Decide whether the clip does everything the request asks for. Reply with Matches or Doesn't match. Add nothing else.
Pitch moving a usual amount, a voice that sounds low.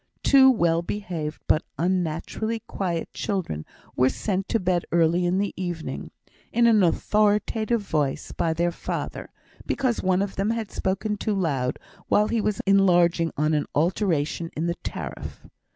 Doesn't match